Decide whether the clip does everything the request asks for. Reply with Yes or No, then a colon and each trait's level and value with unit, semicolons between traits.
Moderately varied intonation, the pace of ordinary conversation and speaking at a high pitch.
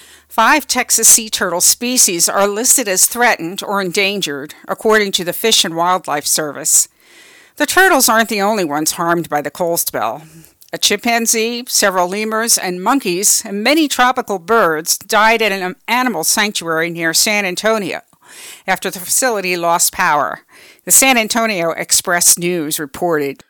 Yes: average, 4.7 semitones; average, 150 wpm; high, 200 Hz